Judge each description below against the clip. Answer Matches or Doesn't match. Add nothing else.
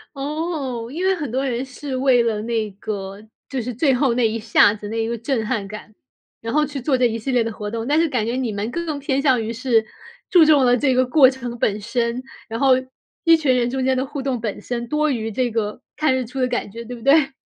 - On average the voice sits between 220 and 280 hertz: Matches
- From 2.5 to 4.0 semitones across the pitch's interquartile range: Matches